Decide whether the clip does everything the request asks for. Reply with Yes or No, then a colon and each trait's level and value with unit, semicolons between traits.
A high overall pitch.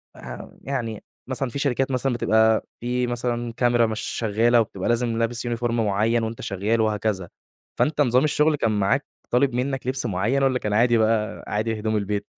No: low, 115 Hz